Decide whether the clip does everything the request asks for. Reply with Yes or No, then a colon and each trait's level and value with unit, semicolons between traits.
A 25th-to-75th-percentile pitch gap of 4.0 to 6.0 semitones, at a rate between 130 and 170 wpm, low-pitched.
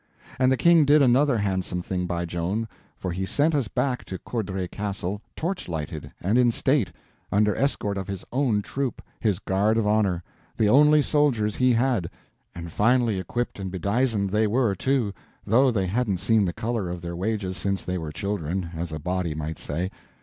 No: average, 5.2 semitones; average, 180 wpm; low, 105 Hz